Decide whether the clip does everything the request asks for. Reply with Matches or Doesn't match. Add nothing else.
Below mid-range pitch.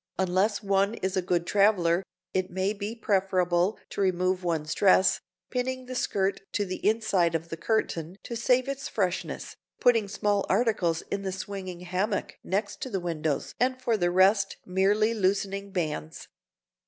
Doesn't match